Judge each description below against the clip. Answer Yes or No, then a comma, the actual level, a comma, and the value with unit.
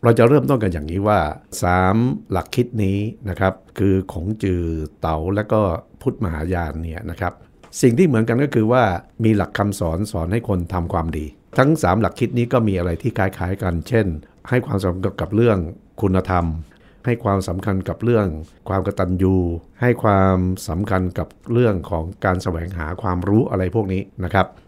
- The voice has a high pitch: No, very low, 95 Hz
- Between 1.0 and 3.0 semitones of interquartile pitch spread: No, average, 3.5 semitones